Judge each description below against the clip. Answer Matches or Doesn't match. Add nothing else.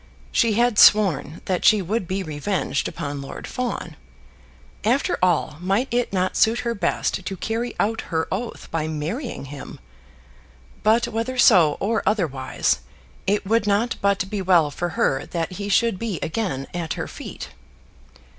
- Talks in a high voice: Matches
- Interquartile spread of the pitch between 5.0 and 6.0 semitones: Matches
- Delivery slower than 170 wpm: Matches